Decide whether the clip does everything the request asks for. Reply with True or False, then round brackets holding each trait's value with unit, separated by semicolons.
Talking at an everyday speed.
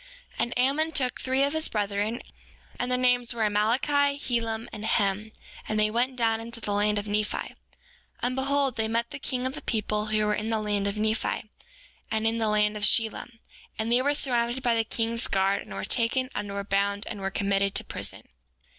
False (215 wpm)